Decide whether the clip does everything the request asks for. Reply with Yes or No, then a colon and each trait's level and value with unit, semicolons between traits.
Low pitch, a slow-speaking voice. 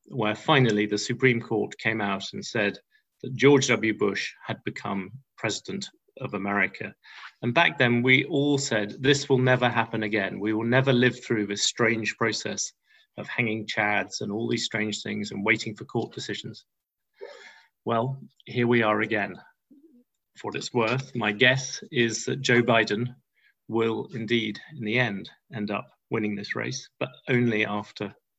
No: low, 115 Hz; average, 165 wpm